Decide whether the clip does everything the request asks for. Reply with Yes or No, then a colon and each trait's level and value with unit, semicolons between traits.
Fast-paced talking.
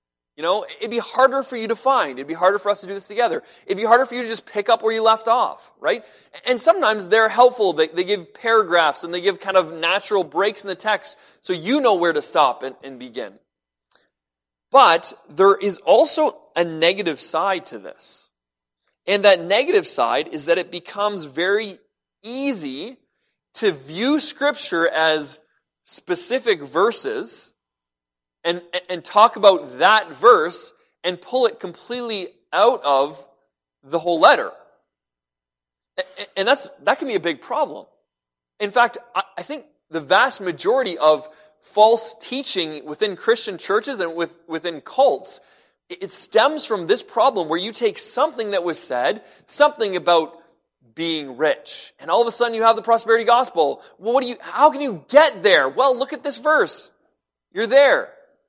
No: average, 170 wpm